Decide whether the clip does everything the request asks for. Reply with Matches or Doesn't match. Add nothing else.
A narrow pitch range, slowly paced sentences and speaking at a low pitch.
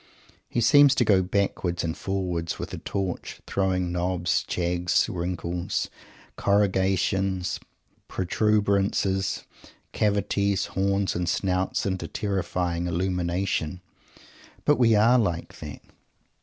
Matches